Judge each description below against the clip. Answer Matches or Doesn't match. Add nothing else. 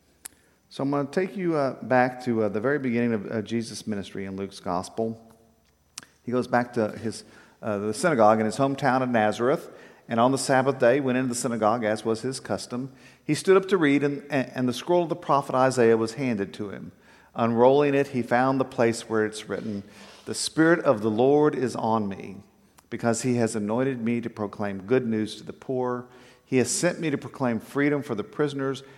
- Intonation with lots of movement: Doesn't match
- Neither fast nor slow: Doesn't match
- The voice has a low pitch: Matches